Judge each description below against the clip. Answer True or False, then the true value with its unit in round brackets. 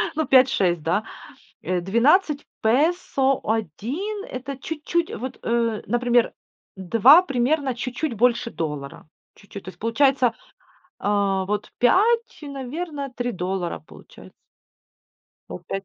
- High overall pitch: True (245 Hz)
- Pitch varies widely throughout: True (5.8 semitones)